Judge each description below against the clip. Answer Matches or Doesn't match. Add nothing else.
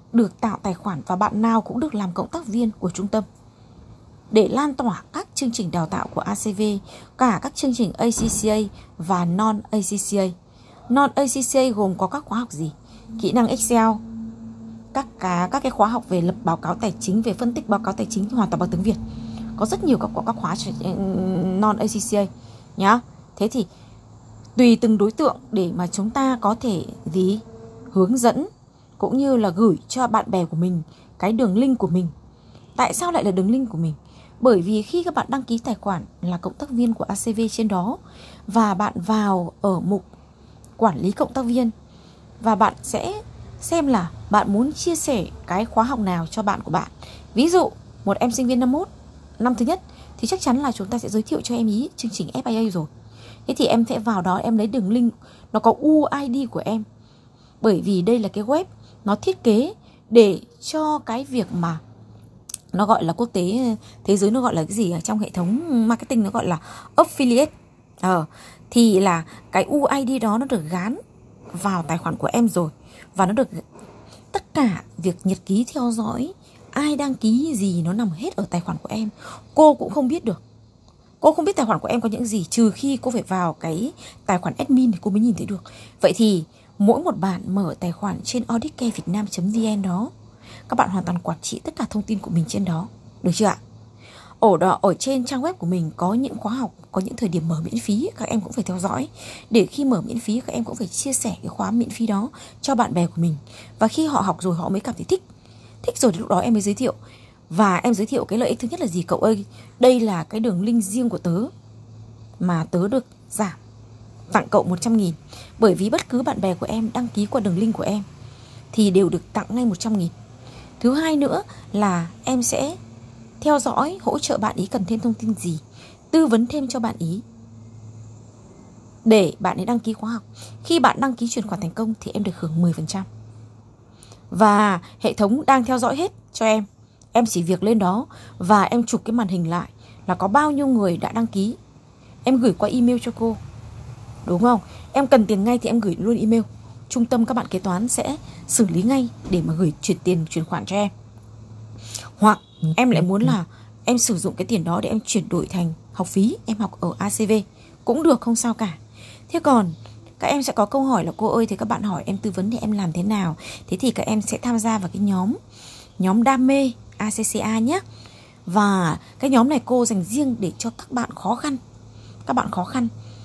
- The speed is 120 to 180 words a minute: Doesn't match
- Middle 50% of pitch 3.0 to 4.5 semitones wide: Doesn't match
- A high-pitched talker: Matches